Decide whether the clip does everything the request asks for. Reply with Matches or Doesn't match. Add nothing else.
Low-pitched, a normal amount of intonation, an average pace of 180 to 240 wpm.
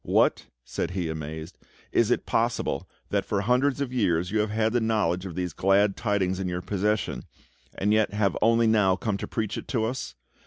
Matches